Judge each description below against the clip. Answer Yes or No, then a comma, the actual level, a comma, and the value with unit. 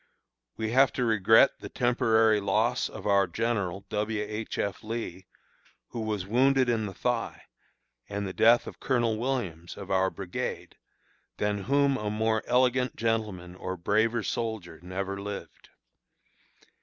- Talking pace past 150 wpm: No, average, 145 wpm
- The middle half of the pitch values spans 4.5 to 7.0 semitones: No, average, 3.2 semitones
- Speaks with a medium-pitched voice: No, low, 110 Hz